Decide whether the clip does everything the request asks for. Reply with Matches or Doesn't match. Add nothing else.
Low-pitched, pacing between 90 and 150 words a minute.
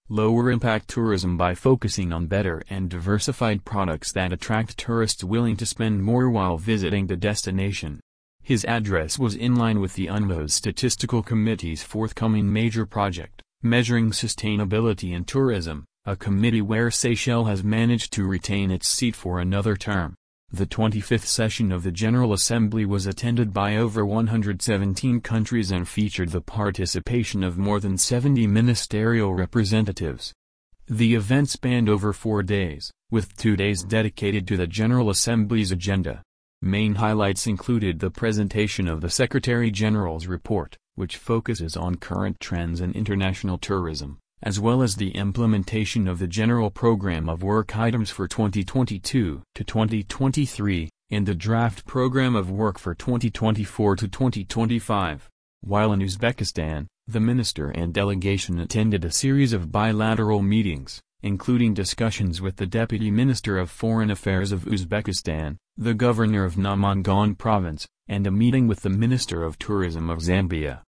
Matches